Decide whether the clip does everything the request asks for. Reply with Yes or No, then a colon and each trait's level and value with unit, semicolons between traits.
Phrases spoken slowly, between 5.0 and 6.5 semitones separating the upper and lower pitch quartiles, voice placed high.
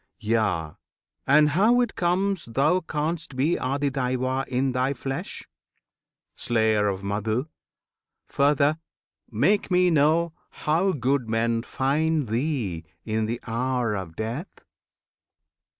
No: slow, 110 wpm; wide, 5.5 semitones; low, 135 Hz